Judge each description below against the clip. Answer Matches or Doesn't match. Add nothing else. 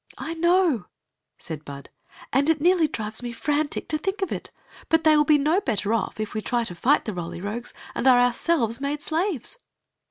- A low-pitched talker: Doesn't match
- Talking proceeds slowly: Doesn't match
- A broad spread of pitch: Matches